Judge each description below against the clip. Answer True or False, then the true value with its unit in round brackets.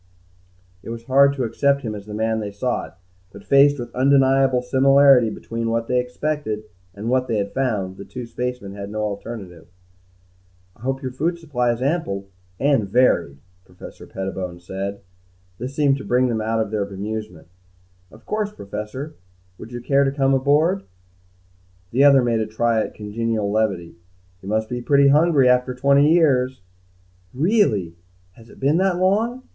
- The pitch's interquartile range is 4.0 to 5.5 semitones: True (4.6 semitones)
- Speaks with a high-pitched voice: False (125 Hz)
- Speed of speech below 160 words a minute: False (170 wpm)